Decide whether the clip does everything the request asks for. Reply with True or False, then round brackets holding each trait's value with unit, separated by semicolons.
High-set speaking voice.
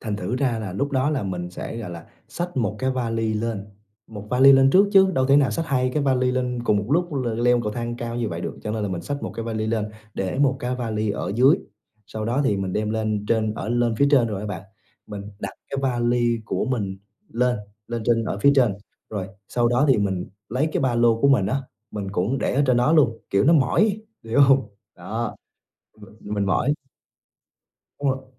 False (120 Hz)